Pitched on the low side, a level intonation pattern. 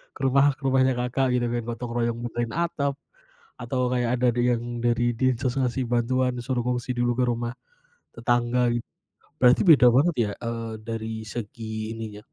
Yes: low, 120 Hz; narrow, 1.6 semitones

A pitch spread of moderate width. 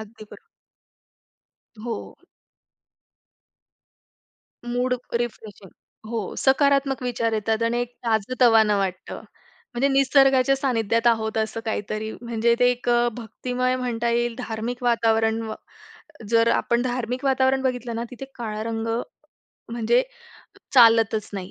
No: narrow, 2.2 semitones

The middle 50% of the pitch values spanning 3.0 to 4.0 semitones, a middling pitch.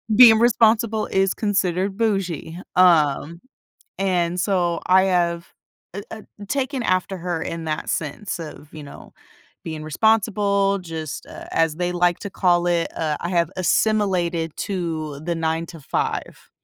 Yes: average, 3.3 semitones; medium, 180 Hz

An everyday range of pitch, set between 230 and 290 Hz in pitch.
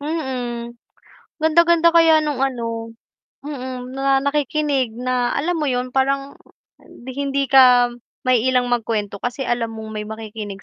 Yes: average, 3.0 semitones; very high, 255 Hz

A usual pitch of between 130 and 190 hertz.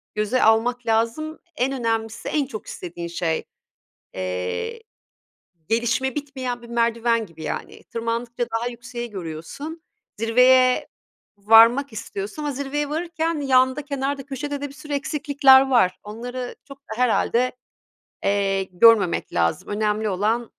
No: high, 240 Hz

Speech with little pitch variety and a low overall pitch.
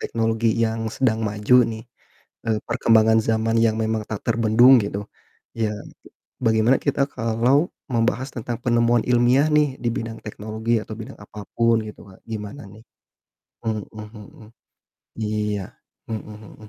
Yes: narrow, 1.6 semitones; low, 110 Hz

